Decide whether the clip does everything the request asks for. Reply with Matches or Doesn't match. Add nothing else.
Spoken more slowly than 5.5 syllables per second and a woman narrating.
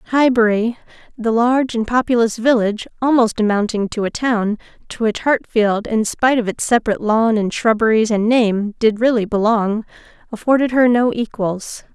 Matches